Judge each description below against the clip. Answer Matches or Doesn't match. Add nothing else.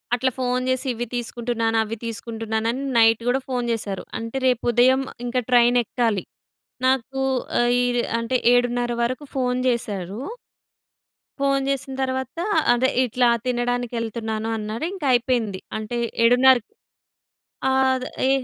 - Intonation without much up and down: Matches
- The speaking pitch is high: Matches